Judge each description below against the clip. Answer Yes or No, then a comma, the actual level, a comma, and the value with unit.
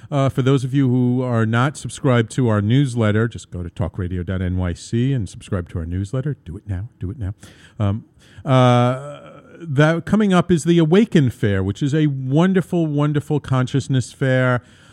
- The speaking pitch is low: Yes, low, 125 Hz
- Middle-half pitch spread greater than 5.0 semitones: Yes, wide, 5.6 semitones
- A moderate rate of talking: Yes, average, 175 wpm